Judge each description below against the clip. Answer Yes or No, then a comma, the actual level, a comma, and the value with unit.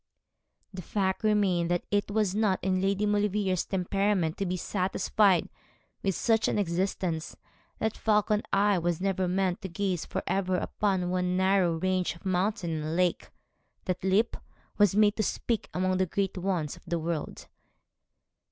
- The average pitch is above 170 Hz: Yes, high, 190 Hz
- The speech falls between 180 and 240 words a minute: No, average, 160 wpm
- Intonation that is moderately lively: No, narrow, 2.2 semitones